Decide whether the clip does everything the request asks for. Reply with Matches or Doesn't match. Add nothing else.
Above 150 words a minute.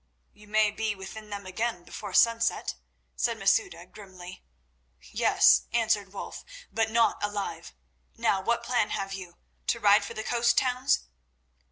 Doesn't match